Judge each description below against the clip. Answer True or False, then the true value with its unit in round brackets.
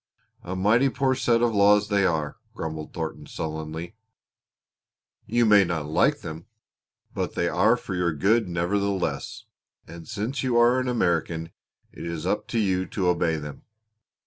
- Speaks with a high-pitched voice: False (95 Hz)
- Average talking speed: True (155 wpm)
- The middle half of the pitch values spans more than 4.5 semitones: True (5.2 semitones)